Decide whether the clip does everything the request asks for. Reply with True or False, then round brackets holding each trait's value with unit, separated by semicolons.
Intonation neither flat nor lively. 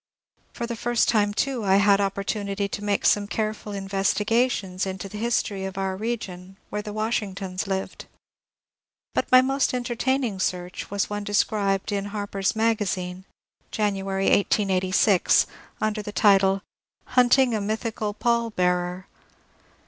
False (2.3 semitones)